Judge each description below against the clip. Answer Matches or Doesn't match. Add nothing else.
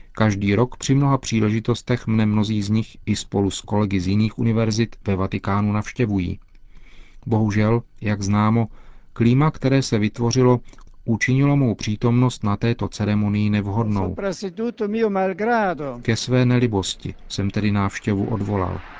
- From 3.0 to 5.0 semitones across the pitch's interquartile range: Matches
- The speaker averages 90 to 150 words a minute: Matches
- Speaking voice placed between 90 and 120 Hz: Matches